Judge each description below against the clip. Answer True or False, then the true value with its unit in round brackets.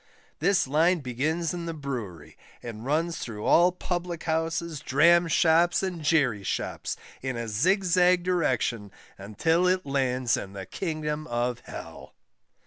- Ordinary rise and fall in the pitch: False (5.7 semitones)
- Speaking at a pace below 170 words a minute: True (135 wpm)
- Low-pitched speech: False (155 Hz)